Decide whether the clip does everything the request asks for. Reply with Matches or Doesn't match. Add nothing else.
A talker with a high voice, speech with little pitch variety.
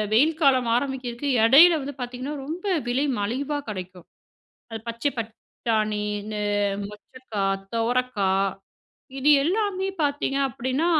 Doesn't match